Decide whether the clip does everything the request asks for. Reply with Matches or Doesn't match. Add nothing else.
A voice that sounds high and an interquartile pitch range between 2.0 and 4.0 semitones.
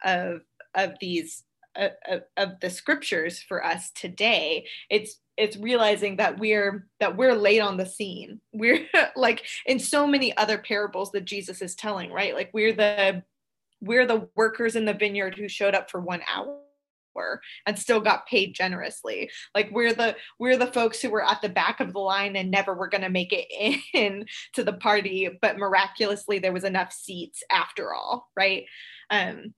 Matches